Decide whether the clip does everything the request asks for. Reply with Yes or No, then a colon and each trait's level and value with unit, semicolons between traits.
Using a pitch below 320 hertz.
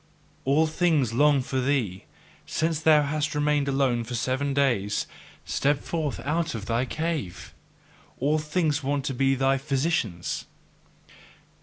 Yes: medium, 140 Hz